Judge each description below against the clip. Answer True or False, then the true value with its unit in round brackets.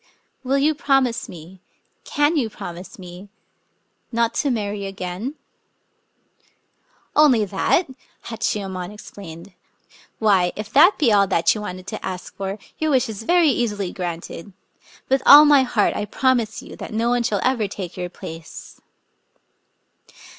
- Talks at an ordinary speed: True (160 wpm)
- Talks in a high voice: True (210 Hz)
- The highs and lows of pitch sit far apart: True (5.7 semitones)